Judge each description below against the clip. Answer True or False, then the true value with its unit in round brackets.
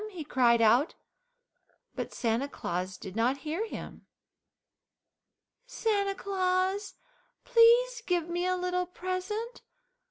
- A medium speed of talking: False (105 wpm)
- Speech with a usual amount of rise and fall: False (7.0 semitones)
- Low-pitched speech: False (360 Hz)